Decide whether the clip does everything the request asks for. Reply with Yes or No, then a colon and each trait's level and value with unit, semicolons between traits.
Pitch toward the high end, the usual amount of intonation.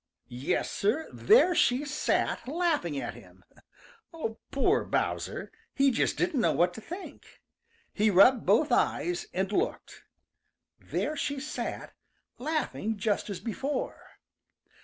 No: very high, 275 Hz; wide, 7.0 semitones